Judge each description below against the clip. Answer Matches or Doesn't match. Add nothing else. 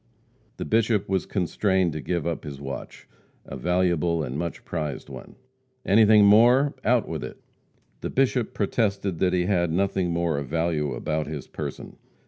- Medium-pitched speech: Doesn't match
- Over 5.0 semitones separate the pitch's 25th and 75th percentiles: Doesn't match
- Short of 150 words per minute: Doesn't match